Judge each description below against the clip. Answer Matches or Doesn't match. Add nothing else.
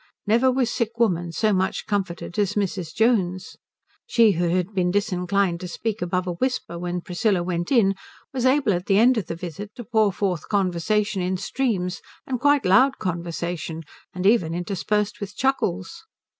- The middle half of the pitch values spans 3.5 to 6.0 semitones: Matches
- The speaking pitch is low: Doesn't match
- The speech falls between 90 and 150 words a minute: Doesn't match